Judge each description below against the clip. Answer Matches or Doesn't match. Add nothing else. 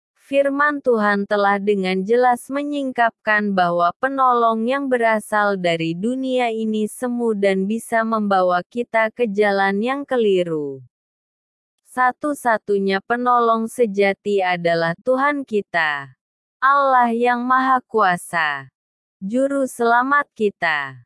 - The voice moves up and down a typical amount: Matches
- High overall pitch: Matches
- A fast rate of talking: Doesn't match